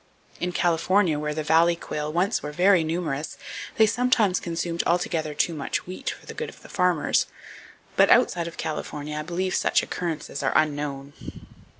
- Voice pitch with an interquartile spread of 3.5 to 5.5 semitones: No, average, 2.9 semitones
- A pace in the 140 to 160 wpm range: No, average, 170 wpm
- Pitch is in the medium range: Yes, medium, 165 Hz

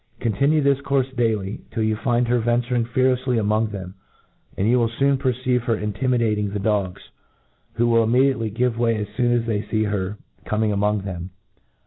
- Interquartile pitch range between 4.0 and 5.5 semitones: No, average, 2.9 semitones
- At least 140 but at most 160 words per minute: No, average, 175 wpm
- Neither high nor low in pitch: No, low, 115 Hz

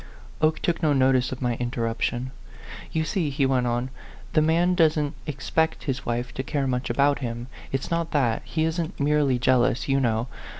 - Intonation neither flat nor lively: Yes, average, 3.9 semitones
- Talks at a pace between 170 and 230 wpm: Yes, average, 190 wpm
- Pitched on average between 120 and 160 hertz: Yes, low, 135 Hz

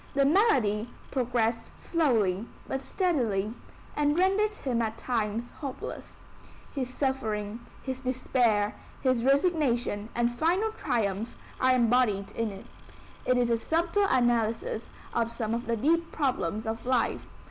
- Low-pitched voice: No, high, 245 Hz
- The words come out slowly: Yes, slow, 130 wpm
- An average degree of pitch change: Yes, average, 4.0 semitones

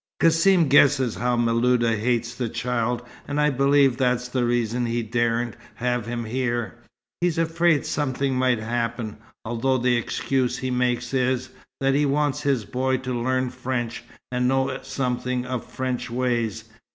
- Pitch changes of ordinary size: No, narrow, 1.9 semitones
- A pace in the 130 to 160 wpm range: Yes, average, 150 wpm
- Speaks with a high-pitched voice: No, low, 125 Hz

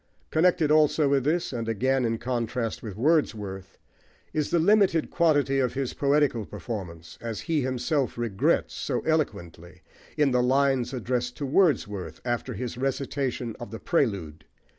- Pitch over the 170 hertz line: No, low, 125 Hz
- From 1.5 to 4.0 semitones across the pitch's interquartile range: No, average, 4.4 semitones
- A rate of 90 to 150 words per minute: Yes, average, 145 wpm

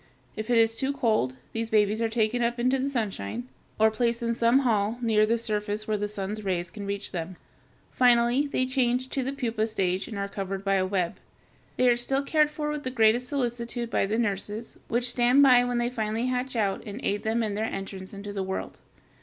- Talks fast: Yes, fast, 220 wpm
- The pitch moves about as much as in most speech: Yes, average, 3.2 semitones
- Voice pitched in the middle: No, high, 225 Hz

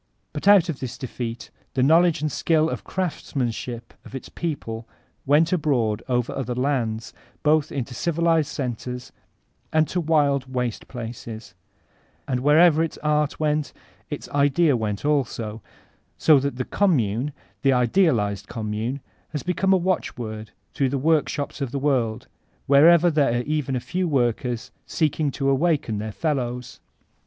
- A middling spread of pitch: Yes, average, 4.4 semitones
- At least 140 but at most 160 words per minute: Yes, average, 145 wpm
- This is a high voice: No, medium, 140 Hz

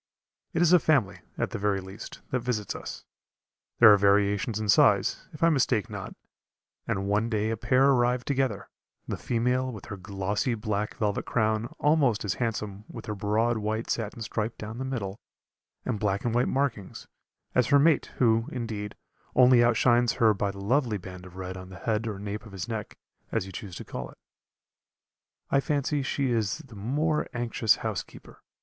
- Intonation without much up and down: No, average, 3.5 semitones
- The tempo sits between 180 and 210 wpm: Yes, average, 185 wpm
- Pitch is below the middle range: Yes, low, 110 Hz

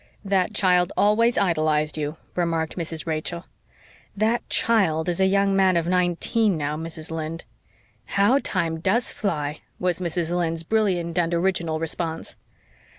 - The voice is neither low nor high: Yes, medium, 175 Hz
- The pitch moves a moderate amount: Yes, average, 3.2 semitones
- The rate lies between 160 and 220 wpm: No, average, 140 wpm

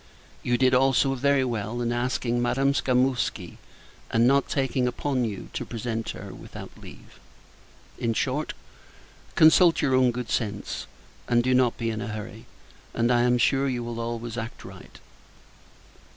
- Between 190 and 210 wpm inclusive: No, average, 155 wpm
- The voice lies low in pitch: Yes, low, 125 Hz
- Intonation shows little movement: Yes, narrow, 2.2 semitones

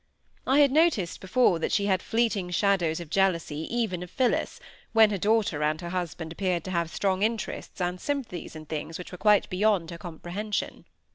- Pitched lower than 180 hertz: No, medium, 185 Hz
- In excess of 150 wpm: Yes, average, 190 wpm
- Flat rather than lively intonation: No, average, 4.0 semitones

